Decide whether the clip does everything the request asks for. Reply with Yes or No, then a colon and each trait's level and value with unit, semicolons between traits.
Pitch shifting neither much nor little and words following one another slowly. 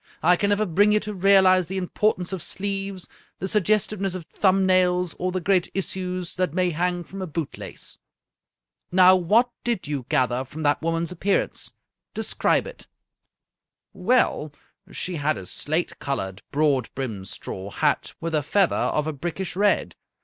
No: average, 3.8 semitones; average, 170 wpm